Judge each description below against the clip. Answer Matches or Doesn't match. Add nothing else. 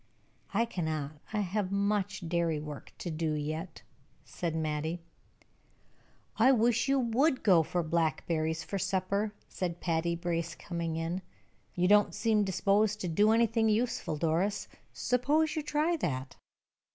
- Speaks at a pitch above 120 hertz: Matches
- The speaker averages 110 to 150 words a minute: Matches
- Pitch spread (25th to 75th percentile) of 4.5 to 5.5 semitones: Matches